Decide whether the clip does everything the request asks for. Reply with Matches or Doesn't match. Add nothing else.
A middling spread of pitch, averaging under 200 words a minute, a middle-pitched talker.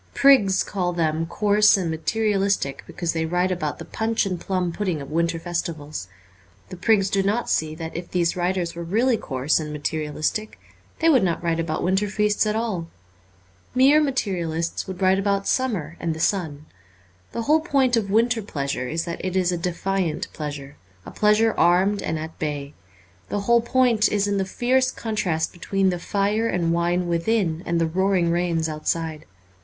Matches